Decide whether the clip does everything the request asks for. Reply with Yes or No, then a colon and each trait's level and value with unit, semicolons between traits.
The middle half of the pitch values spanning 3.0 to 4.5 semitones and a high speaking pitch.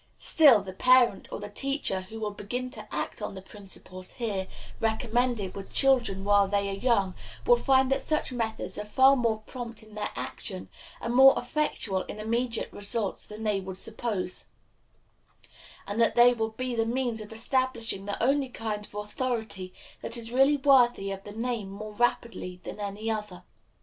Yes: average, 3.5 semitones; high, 220 Hz